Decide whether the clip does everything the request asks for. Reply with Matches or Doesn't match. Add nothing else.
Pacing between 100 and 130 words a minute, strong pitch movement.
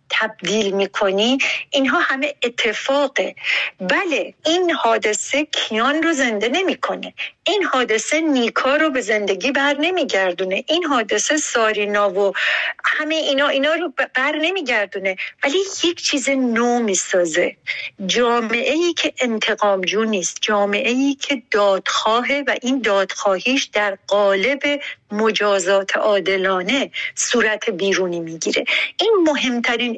Matches